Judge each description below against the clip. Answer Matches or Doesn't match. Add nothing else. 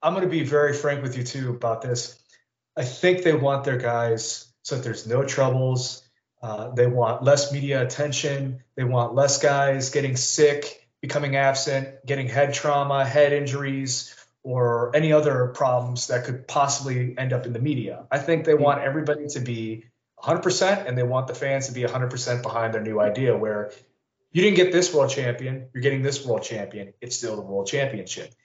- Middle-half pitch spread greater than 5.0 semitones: Doesn't match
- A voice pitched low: Matches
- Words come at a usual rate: Matches